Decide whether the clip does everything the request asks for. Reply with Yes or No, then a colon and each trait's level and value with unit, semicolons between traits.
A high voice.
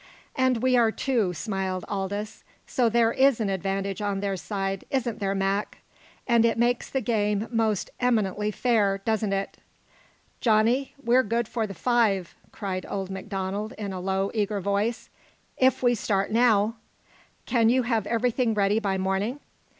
Yes: high, 215 Hz